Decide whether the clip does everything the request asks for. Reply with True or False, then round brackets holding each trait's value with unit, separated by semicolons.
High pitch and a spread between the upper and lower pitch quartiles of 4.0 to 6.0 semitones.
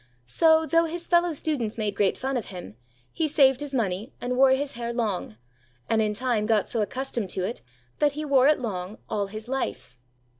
True (245 Hz; 5.2 semitones)